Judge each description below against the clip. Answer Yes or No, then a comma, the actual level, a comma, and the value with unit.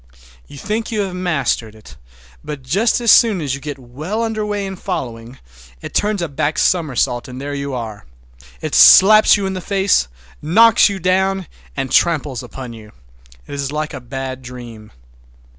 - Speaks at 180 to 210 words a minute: No, average, 170 wpm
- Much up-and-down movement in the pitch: Yes, wide, 7.2 semitones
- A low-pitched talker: No, medium, 150 Hz